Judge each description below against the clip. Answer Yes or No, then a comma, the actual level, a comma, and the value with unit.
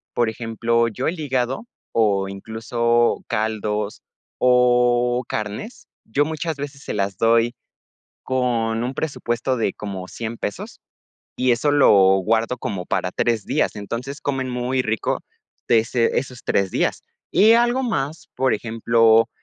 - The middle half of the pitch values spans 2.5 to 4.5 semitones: Yes, average, 2.8 semitones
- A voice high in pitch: No, low, 120 Hz